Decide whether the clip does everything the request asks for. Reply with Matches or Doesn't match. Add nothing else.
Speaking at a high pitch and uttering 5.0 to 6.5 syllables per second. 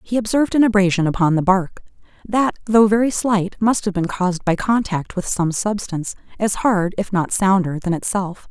Matches